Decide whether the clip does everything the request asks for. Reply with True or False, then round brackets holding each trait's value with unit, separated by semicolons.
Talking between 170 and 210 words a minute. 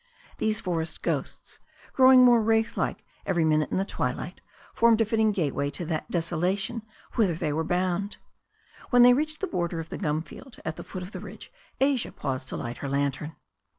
True (195 wpm)